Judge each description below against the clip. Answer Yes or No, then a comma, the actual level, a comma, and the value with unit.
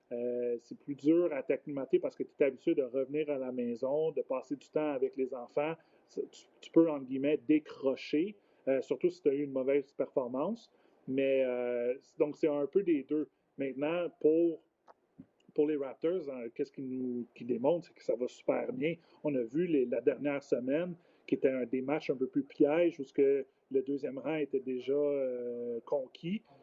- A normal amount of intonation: Yes, average, 3.8 semitones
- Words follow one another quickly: No, average, 195 wpm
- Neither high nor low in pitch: Yes, medium, 145 Hz